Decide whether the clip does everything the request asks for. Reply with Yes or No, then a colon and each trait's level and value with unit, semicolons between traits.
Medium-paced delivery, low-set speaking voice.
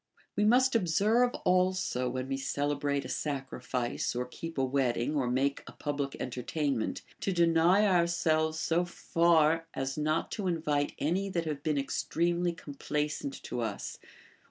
No: average, 160 wpm; medium, 155 Hz